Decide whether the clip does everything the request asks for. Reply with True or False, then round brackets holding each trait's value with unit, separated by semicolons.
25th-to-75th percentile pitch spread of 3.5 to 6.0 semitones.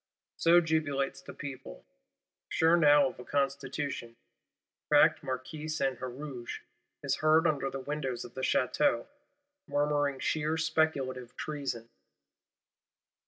False (3.0 semitones)